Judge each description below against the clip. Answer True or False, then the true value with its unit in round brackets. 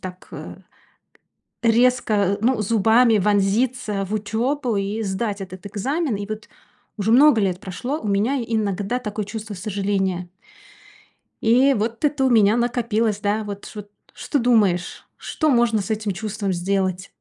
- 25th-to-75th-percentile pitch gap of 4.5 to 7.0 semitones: False (3.1 semitones)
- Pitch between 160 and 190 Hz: False (215 Hz)